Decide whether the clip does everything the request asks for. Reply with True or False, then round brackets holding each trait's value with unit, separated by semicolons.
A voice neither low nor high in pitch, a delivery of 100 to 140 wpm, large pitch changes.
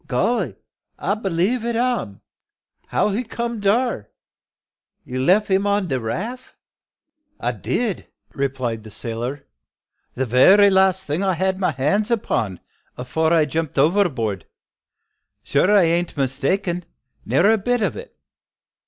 True (180 Hz; 135 wpm; 7.7 semitones)